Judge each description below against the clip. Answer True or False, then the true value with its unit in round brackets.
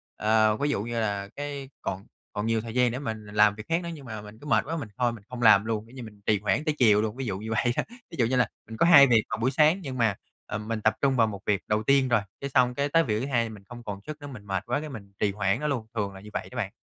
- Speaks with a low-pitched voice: True (115 Hz)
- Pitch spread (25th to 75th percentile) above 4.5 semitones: False (4.2 semitones)